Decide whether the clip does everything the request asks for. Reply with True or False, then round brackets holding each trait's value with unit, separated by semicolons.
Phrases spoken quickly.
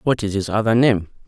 True (235 wpm)